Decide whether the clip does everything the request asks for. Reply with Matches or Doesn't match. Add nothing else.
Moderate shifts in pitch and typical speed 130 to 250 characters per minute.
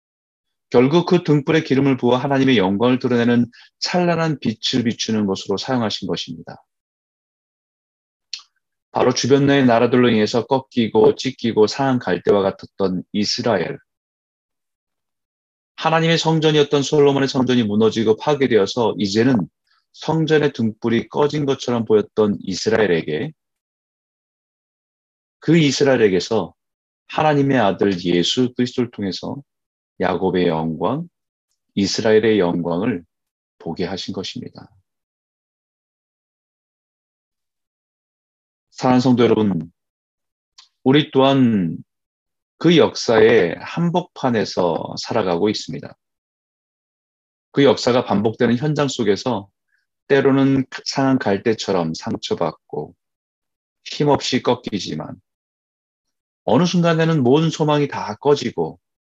Doesn't match